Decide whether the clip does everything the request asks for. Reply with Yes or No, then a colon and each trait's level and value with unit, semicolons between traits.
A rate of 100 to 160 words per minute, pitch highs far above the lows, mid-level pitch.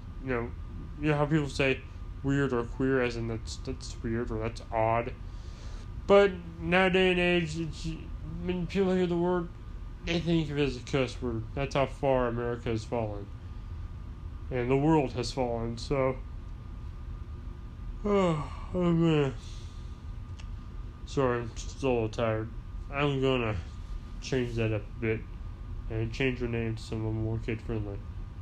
No: average, 150 wpm; wide, 6.3 semitones; low, 115 Hz